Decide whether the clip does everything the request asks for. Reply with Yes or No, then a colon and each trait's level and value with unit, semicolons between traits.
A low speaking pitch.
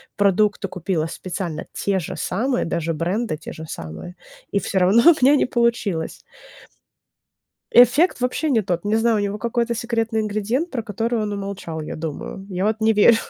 No: high, 205 Hz